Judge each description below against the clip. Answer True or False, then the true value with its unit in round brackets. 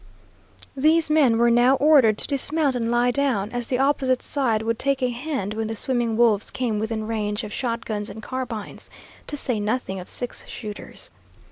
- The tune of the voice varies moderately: True (3.3 semitones)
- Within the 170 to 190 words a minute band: True (180 wpm)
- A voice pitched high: True (240 Hz)